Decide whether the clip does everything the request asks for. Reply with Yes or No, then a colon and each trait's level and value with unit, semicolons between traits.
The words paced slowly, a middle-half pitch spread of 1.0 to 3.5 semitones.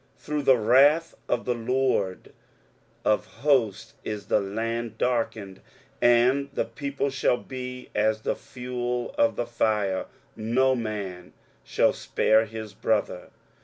Yes: slow, 130 wpm; average, 3.2 semitones